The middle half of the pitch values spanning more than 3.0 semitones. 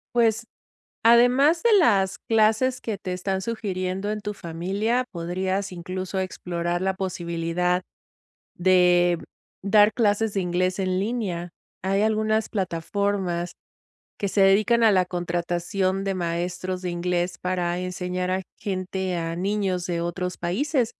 No: average, 2.7 semitones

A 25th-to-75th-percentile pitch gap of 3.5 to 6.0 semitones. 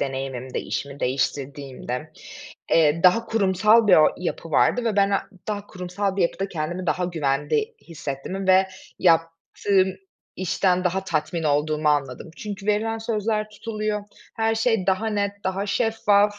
Yes: average, 5.3 semitones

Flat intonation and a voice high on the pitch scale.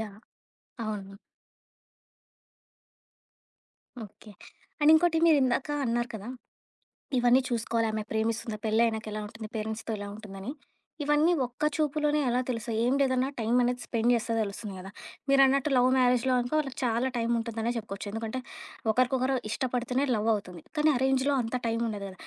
No: average, 3.1 semitones; high, 235 Hz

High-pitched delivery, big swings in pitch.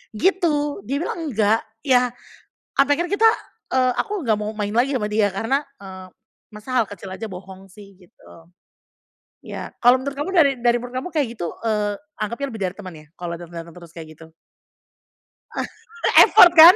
Yes: high, 220 Hz; wide, 6.2 semitones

